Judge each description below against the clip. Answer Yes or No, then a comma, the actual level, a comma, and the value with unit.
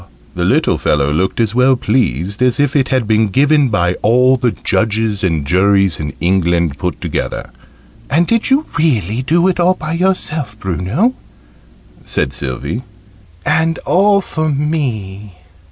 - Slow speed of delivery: No, average, 150 wpm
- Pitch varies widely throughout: Yes, wide, 8.4 semitones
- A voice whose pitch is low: Yes, low, 115 Hz